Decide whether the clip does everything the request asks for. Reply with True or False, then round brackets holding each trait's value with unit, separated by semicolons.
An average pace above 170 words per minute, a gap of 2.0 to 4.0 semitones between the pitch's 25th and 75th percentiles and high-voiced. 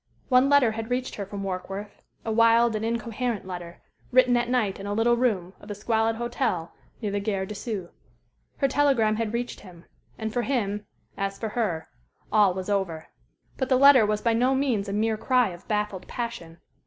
True (195 wpm; 3.3 semitones; 220 Hz)